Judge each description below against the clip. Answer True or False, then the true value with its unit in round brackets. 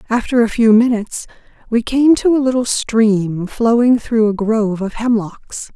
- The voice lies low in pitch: False (225 Hz)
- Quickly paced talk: False (165 wpm)